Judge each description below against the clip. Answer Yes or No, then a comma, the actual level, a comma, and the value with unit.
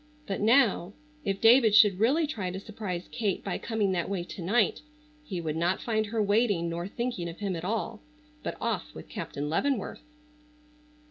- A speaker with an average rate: Yes, average, 180 wpm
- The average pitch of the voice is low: No, high, 200 Hz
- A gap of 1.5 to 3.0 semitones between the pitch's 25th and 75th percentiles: No, average, 4.1 semitones